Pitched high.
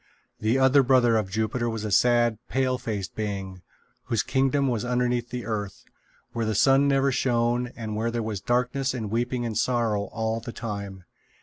No: low, 120 Hz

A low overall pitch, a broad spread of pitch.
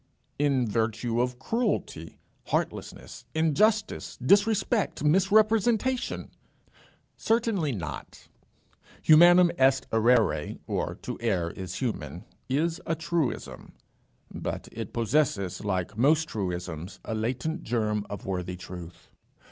Yes: low, 125 Hz; wide, 9.0 semitones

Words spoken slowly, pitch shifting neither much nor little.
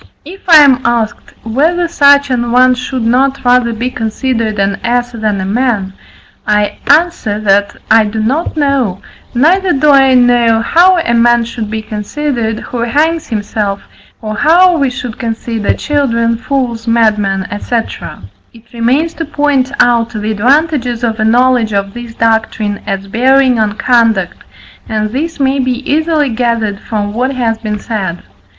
No: average, 155 wpm; average, 3.8 semitones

